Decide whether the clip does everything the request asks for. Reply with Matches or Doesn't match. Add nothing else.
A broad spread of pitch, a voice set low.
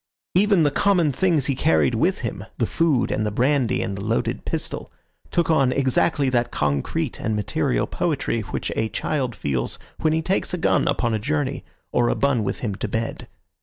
Matches